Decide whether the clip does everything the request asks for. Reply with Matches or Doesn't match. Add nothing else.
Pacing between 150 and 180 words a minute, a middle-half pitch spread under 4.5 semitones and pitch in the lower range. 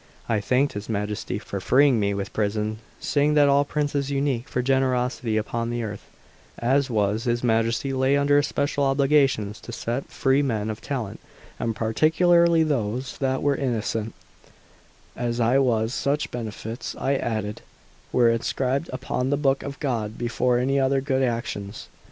Matches